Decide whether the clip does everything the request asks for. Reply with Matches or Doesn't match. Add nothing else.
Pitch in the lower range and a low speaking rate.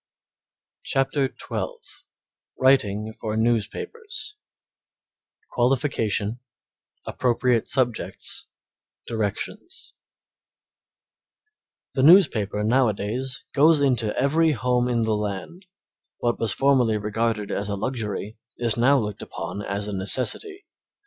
Matches